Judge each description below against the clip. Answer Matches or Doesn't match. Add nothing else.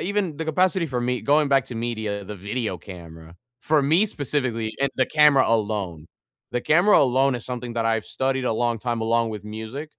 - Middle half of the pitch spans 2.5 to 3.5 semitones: Doesn't match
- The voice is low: Matches